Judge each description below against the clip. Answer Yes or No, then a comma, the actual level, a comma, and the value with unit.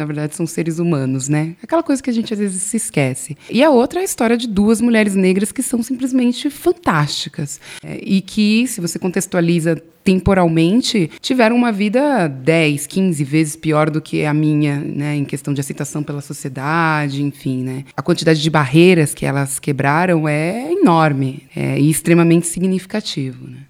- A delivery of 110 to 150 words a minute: No, average, 175 wpm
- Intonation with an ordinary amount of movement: No, wide, 6.2 semitones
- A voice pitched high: No, medium, 165 Hz